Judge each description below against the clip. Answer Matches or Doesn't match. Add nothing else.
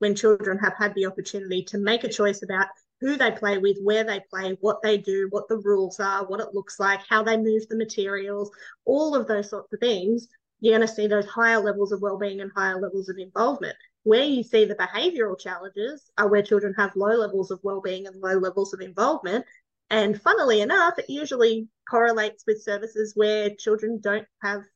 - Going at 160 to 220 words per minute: Matches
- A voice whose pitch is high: Matches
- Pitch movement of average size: Doesn't match